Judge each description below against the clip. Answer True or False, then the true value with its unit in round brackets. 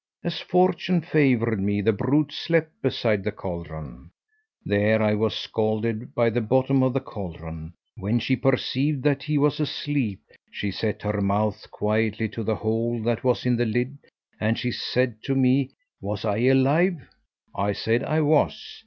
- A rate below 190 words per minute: True (165 wpm)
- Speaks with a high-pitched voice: False (115 Hz)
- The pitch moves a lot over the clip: False (4.3 semitones)